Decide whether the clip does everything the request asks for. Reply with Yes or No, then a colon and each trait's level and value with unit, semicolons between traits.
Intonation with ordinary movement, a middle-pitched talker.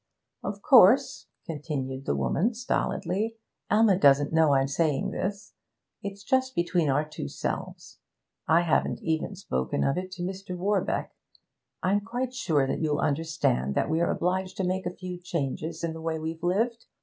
Yes: average, 4.5 semitones; medium, 170 Hz